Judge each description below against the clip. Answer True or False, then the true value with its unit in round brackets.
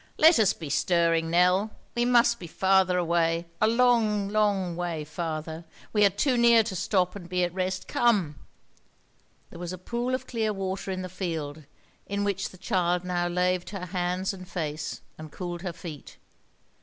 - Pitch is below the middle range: False (185 Hz)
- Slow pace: False (175 wpm)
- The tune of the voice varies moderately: True (3.1 semitones)